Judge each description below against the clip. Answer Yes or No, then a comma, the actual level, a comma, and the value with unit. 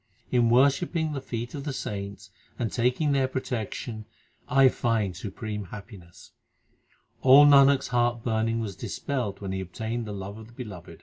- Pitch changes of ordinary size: Yes, average, 4.1 semitones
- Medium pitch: No, low, 115 Hz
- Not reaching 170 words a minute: No, average, 175 wpm